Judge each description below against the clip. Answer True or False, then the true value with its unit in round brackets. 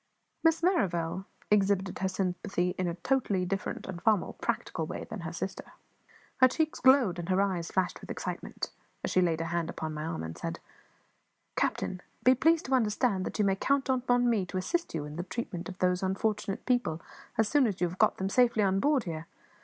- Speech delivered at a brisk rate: True (210 wpm)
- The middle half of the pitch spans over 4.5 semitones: True (5.5 semitones)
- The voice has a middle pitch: False (195 Hz)